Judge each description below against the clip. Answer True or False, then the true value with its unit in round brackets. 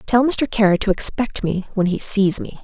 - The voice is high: True (210 Hz)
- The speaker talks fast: True (230 wpm)